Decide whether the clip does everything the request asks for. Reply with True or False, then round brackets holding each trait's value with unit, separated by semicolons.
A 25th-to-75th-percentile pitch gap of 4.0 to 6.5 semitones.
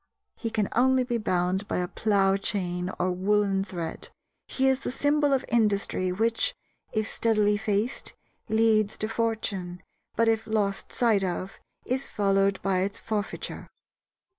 False (2.8 semitones)